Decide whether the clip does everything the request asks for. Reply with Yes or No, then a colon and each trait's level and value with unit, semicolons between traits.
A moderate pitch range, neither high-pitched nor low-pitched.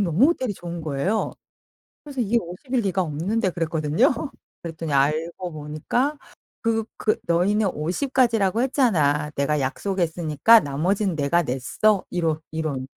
No: wide, 6.1 semitones; medium, 175 Hz